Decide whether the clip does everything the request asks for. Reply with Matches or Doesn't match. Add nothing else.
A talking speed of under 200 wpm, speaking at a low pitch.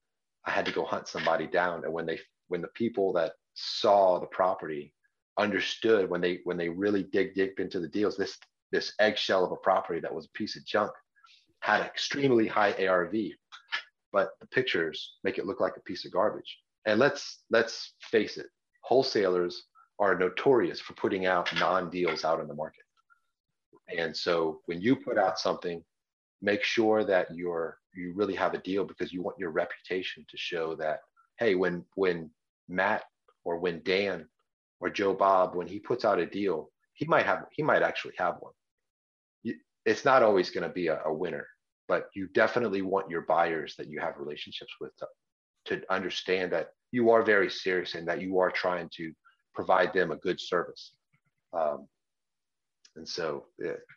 Matches